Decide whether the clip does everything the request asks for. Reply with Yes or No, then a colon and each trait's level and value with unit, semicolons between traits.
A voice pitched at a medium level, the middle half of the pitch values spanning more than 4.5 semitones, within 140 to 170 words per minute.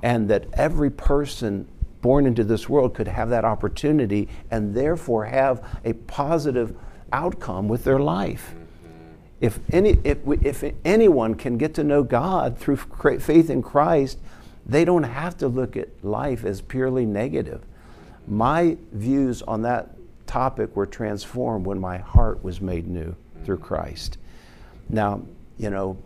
No: low, 115 Hz; average, 5.0 semitones; average, 145 wpm